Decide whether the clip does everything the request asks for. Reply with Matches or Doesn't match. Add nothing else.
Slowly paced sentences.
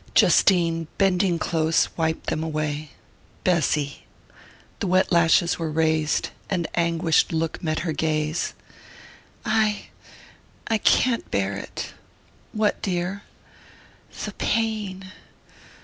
Matches